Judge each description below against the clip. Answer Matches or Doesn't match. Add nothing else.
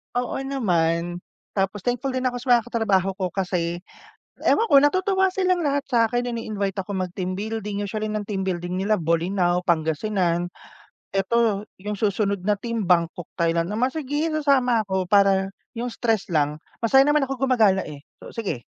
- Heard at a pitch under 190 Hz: Doesn't match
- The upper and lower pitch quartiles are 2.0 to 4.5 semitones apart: Doesn't match